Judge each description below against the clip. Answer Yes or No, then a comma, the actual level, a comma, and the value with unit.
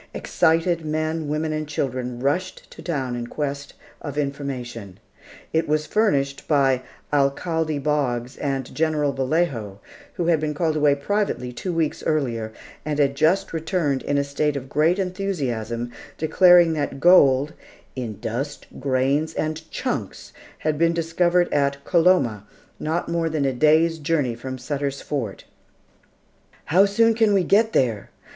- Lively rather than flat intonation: No, average, 3.5 semitones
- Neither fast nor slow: Yes, average, 145 wpm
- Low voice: No, medium, 150 Hz